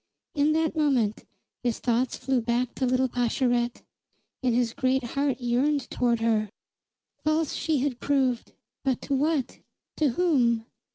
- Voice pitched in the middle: No, very high, 255 Hz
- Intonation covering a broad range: No, average, 3.1 semitones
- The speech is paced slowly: No, average, 145 wpm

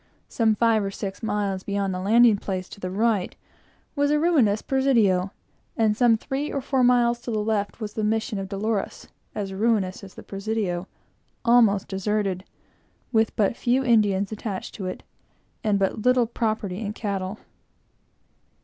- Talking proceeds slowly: No, average, 160 wpm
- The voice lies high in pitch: Yes, high, 215 Hz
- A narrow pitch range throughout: No, average, 3.0 semitones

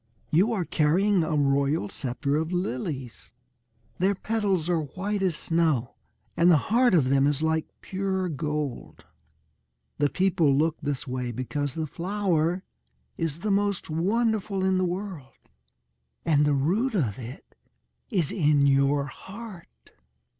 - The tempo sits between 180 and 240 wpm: No, average, 140 wpm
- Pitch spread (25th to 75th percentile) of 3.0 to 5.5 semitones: Yes, average, 5.1 semitones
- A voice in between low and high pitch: Yes, medium, 160 Hz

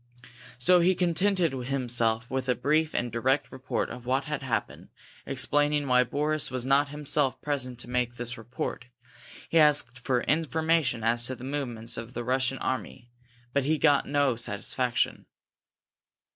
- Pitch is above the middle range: No, low, 130 Hz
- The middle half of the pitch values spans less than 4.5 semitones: Yes, average, 3.3 semitones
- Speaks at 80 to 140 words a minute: No, average, 150 wpm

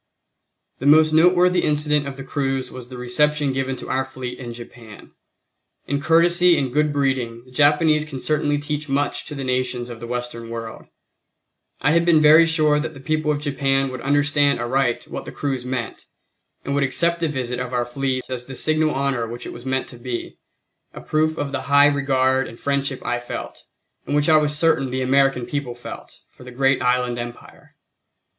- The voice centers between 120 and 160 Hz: Yes, low, 135 Hz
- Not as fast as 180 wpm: No, average, 195 wpm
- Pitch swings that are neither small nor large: Yes, average, 3.0 semitones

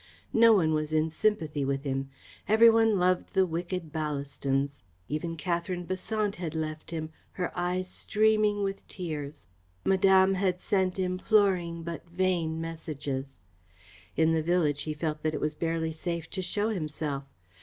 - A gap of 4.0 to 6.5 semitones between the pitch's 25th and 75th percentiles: No, average, 3.4 semitones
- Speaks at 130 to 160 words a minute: Yes, average, 150 wpm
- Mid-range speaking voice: Yes, medium, 170 Hz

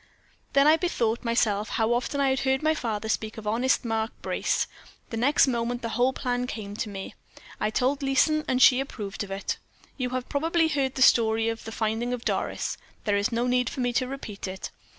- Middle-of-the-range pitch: No, high, 245 Hz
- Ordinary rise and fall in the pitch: Yes, average, 3.2 semitones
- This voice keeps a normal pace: No, fast, 210 wpm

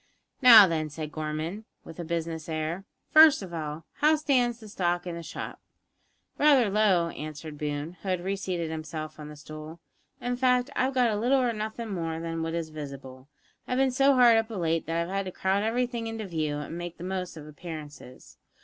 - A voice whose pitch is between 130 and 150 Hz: No, medium, 175 Hz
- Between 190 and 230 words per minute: Yes, average, 200 wpm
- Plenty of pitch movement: Yes, wide, 6.2 semitones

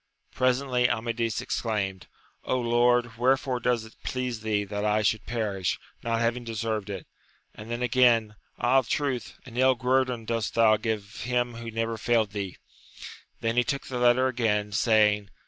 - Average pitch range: No, narrow, 2.3 semitones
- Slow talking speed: No, average, 160 wpm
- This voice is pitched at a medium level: No, low, 115 Hz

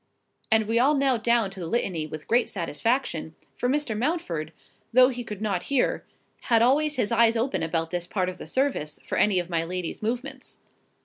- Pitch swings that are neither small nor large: No, wide, 6.2 semitones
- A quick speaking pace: No, average, 195 wpm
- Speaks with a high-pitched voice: Yes, high, 225 Hz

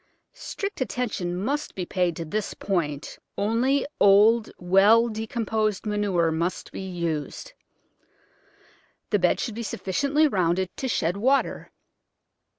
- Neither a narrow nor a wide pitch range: Yes, average, 4.5 semitones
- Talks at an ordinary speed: No, slow, 120 wpm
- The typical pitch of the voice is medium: No, high, 205 Hz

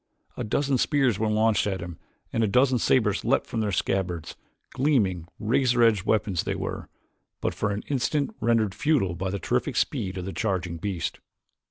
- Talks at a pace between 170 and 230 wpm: Yes, average, 180 wpm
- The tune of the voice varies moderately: Yes, average, 4.6 semitones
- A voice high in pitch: No, low, 105 Hz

